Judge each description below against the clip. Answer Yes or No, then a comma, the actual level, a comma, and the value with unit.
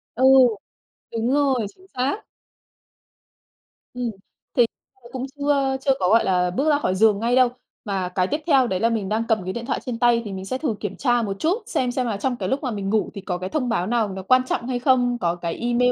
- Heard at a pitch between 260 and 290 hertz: No, high, 235 Hz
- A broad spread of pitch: No, average, 4.6 semitones